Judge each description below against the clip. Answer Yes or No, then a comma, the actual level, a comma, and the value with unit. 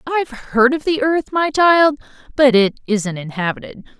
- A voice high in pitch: Yes, very high, 265 Hz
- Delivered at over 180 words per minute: No, average, 165 wpm